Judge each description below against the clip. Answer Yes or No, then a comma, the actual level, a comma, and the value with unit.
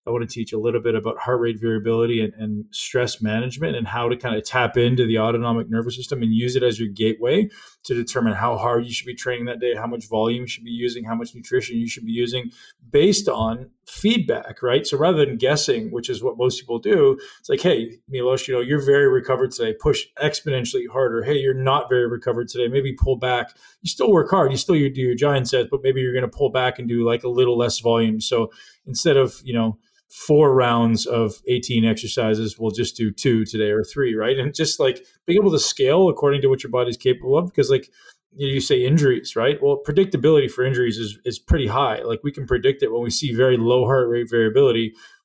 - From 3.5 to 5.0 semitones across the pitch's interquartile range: No, average, 3.1 semitones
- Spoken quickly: Yes, fast, 230 wpm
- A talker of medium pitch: No, low, 125 Hz